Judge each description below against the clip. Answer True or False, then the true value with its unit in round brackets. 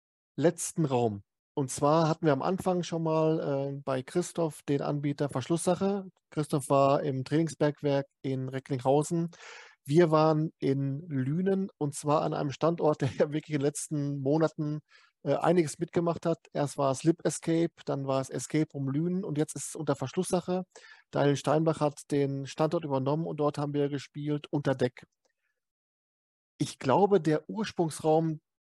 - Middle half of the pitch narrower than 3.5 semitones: True (3.0 semitones)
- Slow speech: False (155 wpm)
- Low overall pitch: False (150 Hz)